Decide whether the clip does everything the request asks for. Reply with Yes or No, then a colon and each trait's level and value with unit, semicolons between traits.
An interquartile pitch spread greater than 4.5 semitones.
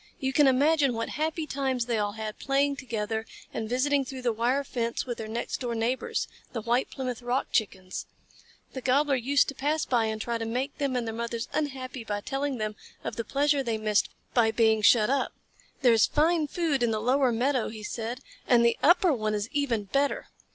No: average, 3.6 semitones